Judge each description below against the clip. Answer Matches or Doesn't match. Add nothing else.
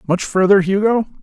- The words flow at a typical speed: Matches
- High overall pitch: Matches